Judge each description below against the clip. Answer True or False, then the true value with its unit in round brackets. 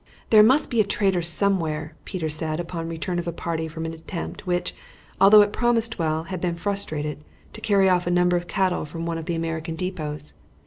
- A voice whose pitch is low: False (175 Hz)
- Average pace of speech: False (215 wpm)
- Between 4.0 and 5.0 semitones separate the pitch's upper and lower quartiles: False (3.1 semitones)